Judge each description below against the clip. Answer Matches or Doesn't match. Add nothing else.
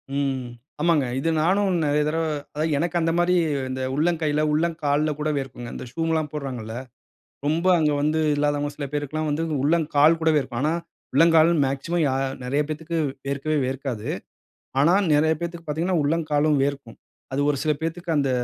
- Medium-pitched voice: Matches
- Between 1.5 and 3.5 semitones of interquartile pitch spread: Matches